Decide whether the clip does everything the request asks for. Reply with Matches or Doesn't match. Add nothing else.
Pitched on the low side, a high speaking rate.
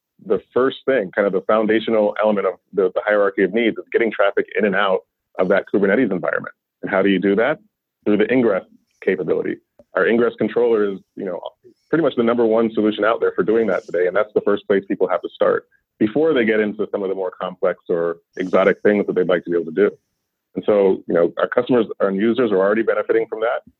Matches